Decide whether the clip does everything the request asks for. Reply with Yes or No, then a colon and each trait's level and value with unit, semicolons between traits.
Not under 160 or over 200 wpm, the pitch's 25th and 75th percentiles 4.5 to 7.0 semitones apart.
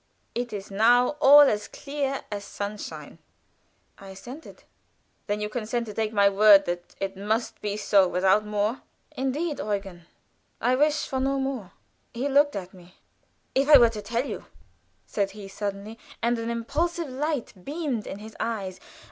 Yes: average, 165 wpm; average, 4.9 semitones